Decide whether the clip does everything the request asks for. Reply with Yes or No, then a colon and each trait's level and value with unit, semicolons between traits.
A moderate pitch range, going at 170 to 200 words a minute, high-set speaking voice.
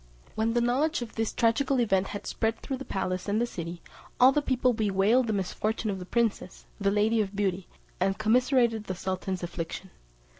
Yes: average, 3.9 semitones; average, 190 wpm; high, 215 Hz